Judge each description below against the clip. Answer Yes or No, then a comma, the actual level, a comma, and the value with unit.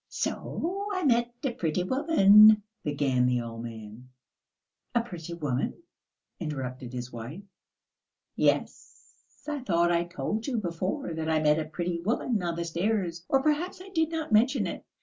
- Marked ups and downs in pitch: Yes, wide, 8.0 semitones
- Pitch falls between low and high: Yes, medium, 175 Hz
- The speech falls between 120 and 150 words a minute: No, average, 160 wpm